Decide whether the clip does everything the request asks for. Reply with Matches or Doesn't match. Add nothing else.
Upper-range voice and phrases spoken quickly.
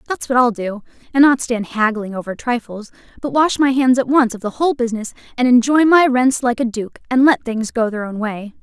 Matches